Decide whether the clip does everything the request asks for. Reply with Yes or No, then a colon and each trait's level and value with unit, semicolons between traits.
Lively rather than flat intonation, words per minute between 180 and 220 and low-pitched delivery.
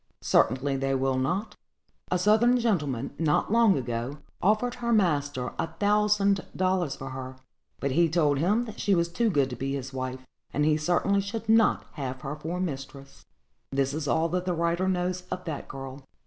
No: wide, 6.4 semitones; average, 190 wpm; medium, 165 Hz